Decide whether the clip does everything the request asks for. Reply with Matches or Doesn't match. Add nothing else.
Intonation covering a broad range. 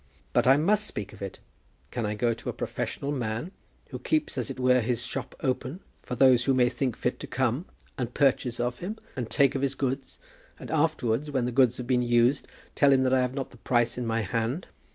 Doesn't match